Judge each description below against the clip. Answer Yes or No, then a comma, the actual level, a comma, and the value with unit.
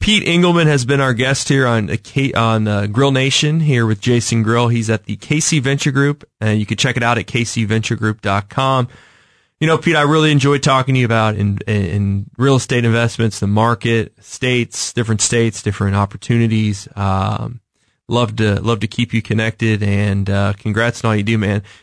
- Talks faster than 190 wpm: No, average, 185 wpm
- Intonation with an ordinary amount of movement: Yes, average, 3.8 semitones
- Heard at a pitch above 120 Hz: No, low, 115 Hz